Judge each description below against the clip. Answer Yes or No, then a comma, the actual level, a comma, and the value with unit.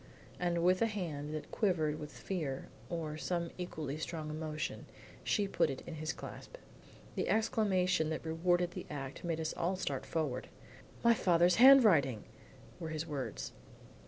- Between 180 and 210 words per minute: No, average, 155 wpm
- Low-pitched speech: No, medium, 165 Hz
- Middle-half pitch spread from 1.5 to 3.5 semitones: Yes, average, 3.0 semitones